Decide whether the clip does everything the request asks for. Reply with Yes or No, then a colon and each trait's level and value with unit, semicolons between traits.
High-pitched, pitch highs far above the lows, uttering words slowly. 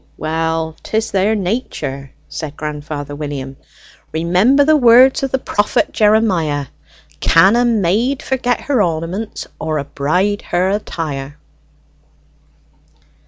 No: medium, 180 Hz; wide, 6.6 semitones; slow, 115 wpm